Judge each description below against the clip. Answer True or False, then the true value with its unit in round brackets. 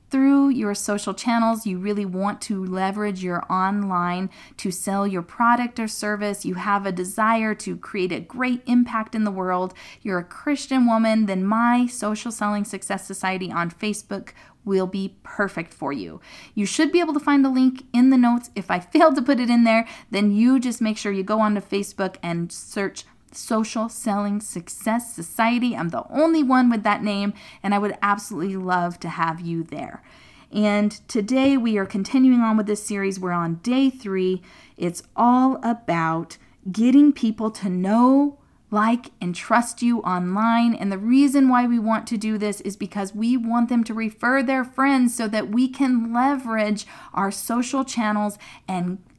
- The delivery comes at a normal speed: True (180 wpm)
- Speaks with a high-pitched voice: True (215 Hz)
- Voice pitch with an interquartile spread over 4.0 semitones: False (3.6 semitones)